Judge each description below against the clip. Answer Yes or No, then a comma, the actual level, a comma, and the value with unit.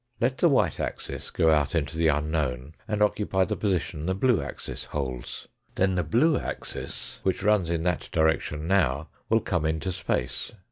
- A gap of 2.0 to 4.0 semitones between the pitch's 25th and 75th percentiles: No, average, 4.4 semitones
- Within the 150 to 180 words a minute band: Yes, average, 175 wpm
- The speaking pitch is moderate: No, very low, 85 Hz